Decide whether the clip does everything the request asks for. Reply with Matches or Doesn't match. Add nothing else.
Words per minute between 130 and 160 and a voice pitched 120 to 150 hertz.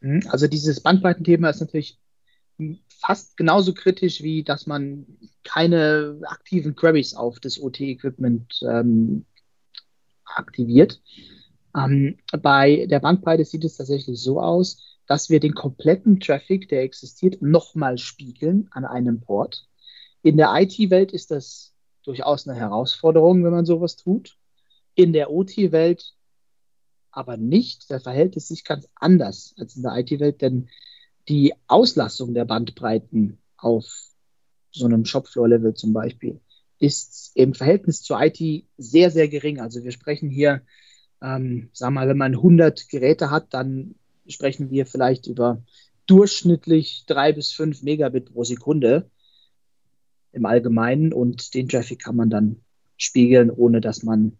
Matches